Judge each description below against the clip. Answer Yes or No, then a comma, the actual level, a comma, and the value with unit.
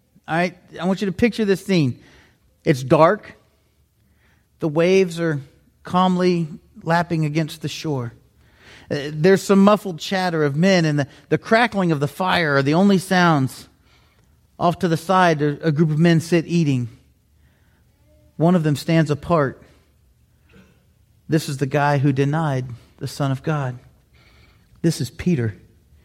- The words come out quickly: No, average, 145 wpm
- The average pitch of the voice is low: No, medium, 160 Hz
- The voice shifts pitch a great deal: No, average, 4.2 semitones